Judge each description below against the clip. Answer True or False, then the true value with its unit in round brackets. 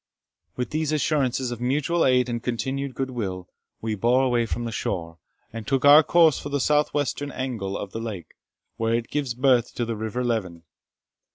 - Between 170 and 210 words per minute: True (190 wpm)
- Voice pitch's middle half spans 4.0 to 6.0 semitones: False (3.4 semitones)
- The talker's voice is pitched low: True (125 Hz)